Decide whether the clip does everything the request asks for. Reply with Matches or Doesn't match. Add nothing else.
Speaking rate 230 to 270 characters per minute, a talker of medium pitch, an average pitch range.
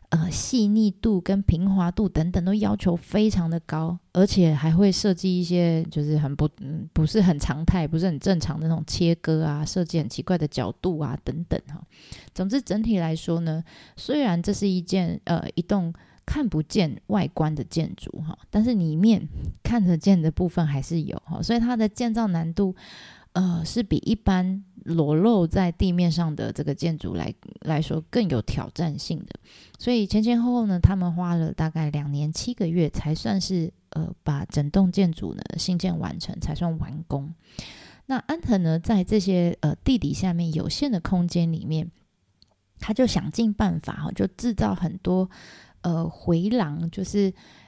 Matches